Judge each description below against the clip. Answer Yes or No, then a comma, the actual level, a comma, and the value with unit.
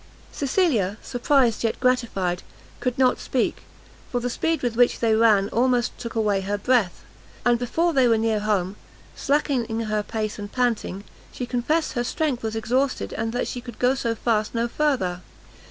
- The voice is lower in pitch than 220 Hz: No, high, 235 Hz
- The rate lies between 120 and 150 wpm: No, average, 170 wpm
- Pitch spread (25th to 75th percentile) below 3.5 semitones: Yes, average, 2.8 semitones